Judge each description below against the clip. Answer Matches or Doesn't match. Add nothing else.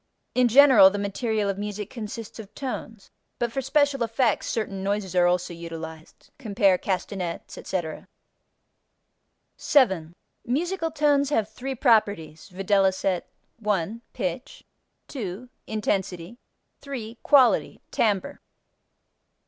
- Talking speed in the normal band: Doesn't match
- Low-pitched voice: Doesn't match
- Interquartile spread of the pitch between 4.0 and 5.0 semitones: Matches